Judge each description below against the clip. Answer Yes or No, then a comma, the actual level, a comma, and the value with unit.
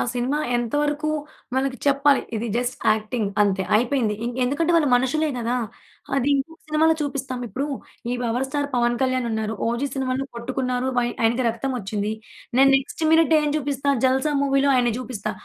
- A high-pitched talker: Yes, very high, 260 Hz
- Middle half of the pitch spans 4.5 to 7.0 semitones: No, average, 2.9 semitones